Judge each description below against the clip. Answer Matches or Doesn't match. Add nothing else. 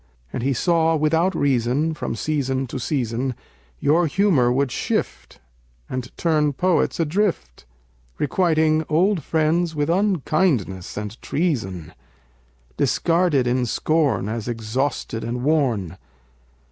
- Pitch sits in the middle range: Matches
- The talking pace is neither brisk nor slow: Doesn't match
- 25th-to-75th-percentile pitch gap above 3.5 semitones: Matches